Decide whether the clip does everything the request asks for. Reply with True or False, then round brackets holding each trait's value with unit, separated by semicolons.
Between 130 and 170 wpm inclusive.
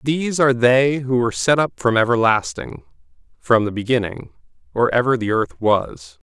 True (160 wpm)